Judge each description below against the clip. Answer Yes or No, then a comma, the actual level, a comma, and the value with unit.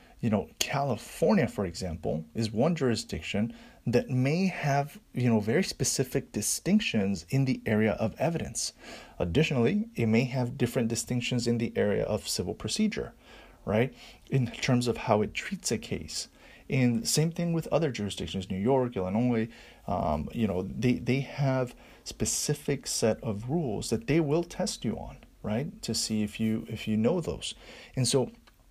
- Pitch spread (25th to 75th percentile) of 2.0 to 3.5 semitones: No, average, 4.3 semitones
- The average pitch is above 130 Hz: No, low, 125 Hz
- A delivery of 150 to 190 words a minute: Yes, average, 165 wpm